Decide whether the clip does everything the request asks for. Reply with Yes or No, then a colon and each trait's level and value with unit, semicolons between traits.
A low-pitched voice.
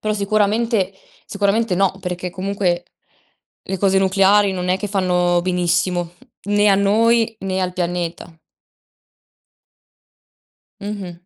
No: high, 190 Hz